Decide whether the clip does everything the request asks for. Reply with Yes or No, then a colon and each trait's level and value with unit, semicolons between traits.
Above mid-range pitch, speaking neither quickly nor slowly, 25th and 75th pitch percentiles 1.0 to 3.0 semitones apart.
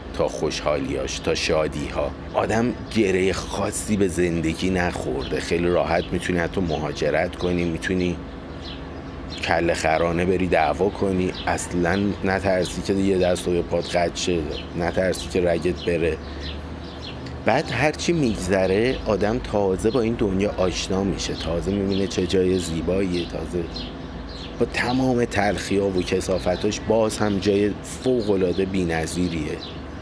No: very low, 90 Hz; average, 125 wpm; narrow, 2.5 semitones